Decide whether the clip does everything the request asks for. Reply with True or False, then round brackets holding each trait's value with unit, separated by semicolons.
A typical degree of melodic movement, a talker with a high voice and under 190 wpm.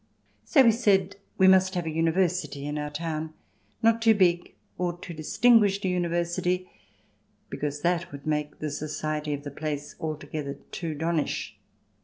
False (3.6 semitones; 170 Hz; 165 wpm)